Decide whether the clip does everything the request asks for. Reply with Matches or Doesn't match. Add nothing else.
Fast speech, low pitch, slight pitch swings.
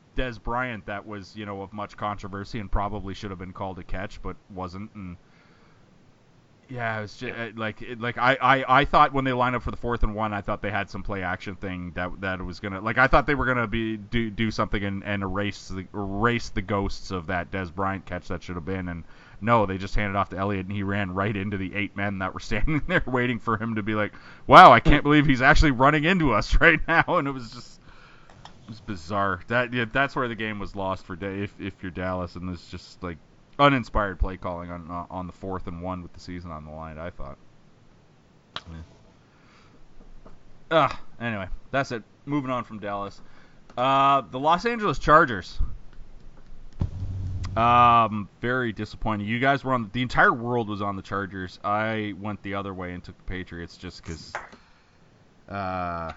Doesn't match